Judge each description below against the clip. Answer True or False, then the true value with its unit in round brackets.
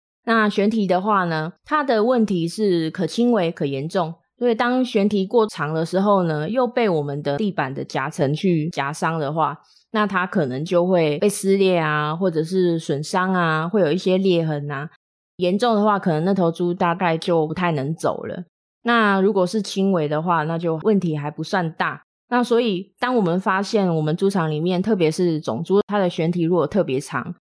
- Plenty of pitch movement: False (4.4 semitones)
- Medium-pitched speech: True (180 Hz)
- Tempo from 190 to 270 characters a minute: False (280 characters per minute)